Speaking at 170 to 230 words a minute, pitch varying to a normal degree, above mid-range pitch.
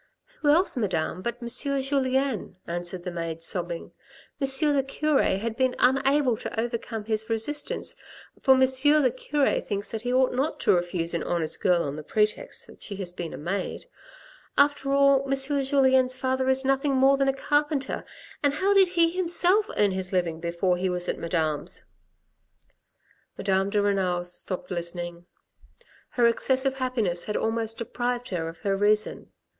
No: average, 180 wpm; wide, 6.9 semitones; high, 235 Hz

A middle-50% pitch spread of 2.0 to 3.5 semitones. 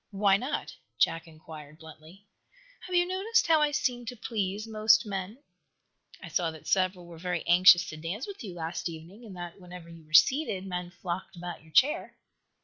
No: average, 5.0 semitones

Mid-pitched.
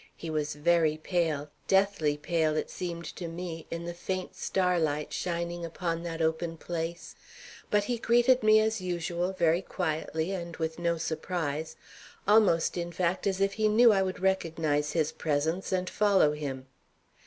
Yes: medium, 170 Hz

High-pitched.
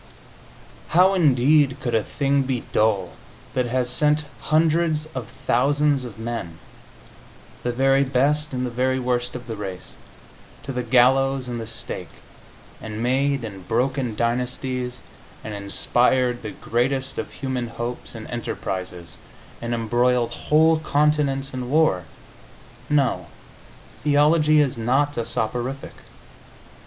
No: low, 125 Hz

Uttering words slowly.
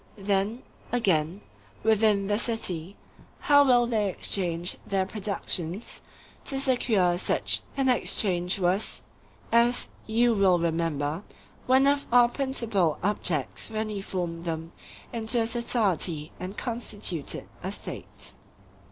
Yes: slow, 115 wpm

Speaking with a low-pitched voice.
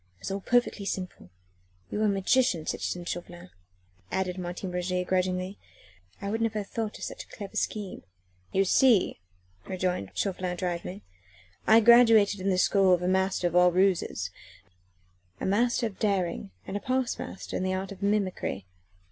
No: high, 190 Hz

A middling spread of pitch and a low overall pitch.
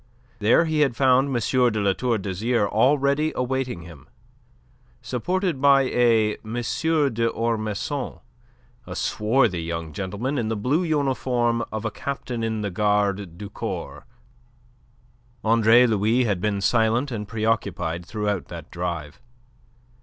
Yes: average, 4.0 semitones; low, 115 Hz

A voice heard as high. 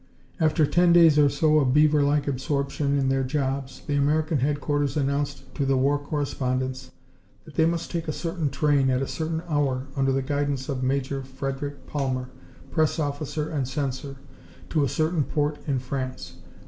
No: medium, 140 Hz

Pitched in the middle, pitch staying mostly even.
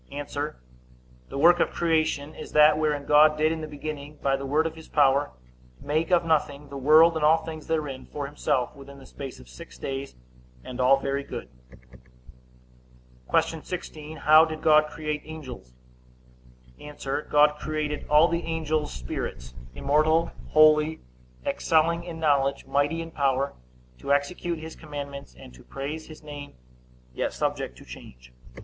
Yes: medium, 150 Hz; narrow, 2.1 semitones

